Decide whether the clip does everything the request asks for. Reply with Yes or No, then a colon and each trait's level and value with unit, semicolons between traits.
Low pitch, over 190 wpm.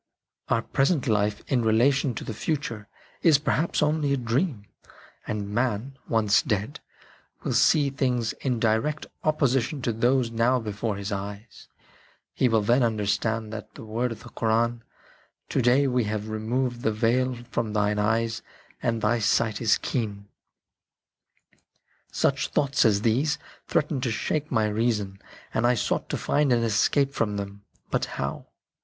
No: low, 115 Hz; average, 155 wpm